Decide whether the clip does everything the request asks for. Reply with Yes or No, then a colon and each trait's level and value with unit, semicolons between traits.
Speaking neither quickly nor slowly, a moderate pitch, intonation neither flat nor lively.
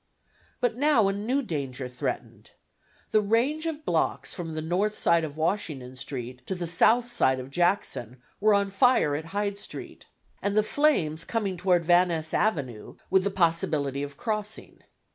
No: average, 165 wpm; medium, 180 Hz; wide, 6.0 semitones